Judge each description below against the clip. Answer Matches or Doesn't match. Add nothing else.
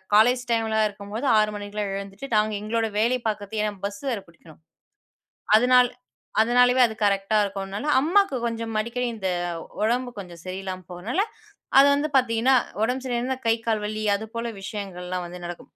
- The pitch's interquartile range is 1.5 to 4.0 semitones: Matches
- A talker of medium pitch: Doesn't match